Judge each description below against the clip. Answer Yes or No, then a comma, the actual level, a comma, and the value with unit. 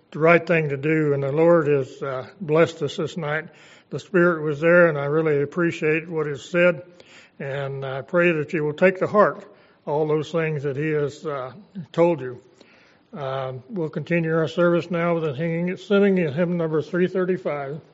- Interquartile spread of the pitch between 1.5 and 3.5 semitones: Yes, average, 2.9 semitones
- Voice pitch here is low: No, medium, 160 Hz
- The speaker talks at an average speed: Yes, average, 185 wpm